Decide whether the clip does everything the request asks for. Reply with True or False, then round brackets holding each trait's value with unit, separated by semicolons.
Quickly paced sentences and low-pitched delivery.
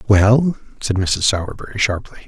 False (130 wpm; 105 Hz)